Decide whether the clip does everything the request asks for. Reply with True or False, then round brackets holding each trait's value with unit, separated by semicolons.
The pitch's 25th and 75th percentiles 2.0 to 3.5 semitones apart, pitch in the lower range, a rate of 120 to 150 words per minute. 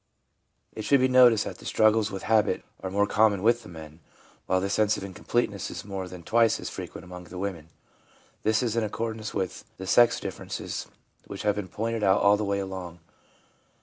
False (2.9 semitones; 100 Hz; 205 wpm)